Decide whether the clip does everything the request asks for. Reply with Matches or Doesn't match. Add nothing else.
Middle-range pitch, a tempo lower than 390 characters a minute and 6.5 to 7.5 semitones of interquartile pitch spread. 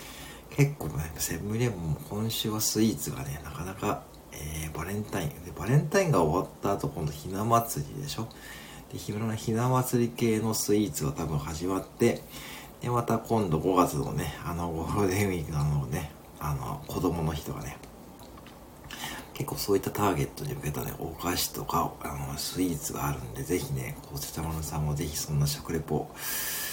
Doesn't match